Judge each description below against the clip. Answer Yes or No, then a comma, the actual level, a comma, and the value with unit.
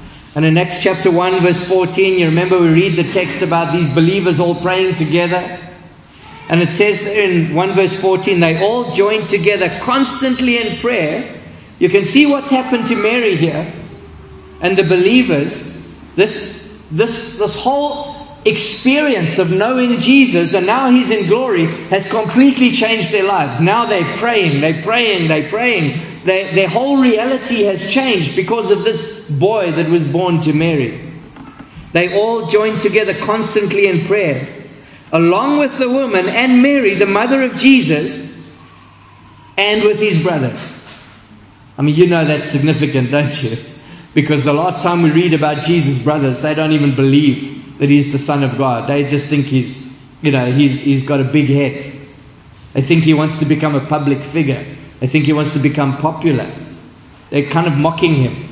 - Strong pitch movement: Yes, wide, 5.9 semitones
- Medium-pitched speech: Yes, medium, 175 Hz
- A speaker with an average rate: Yes, average, 170 wpm